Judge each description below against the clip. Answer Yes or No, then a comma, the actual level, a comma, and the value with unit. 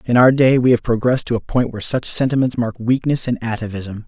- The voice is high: No, low, 120 Hz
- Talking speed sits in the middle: No, fast, 235 wpm